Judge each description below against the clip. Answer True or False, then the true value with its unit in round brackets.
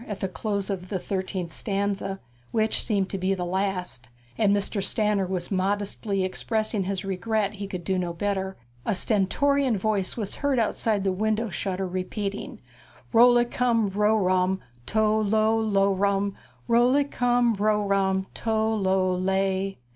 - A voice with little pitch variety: True (2.3 semitones)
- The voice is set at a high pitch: True (200 Hz)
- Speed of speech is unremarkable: True (160 wpm)